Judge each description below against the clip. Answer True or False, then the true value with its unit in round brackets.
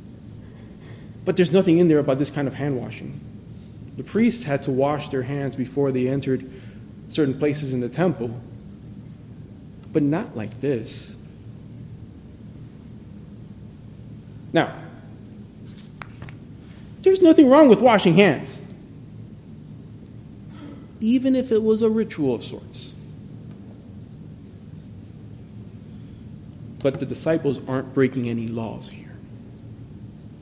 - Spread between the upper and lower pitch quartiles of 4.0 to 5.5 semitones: True (4.6 semitones)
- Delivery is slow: True (105 wpm)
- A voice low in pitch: True (130 Hz)